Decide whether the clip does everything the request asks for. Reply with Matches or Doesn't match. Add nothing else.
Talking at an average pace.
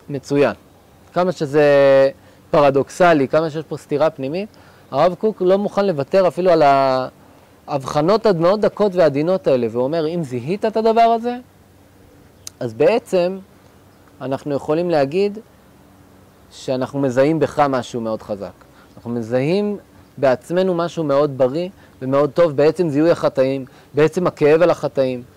Matches